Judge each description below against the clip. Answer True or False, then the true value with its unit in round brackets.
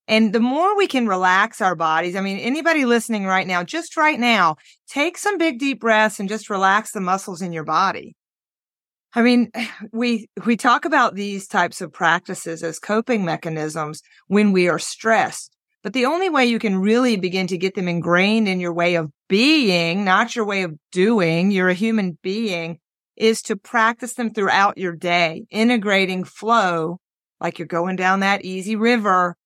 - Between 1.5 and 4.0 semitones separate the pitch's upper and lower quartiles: False (4.5 semitones)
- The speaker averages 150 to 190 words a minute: True (180 wpm)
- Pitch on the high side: True (200 Hz)